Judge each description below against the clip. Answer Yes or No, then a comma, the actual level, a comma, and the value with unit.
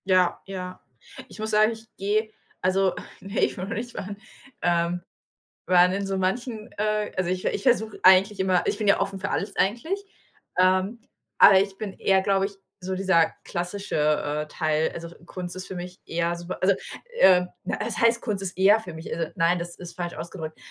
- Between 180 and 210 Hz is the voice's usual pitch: Yes, high, 190 Hz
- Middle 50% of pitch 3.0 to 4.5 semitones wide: No, narrow, 2.5 semitones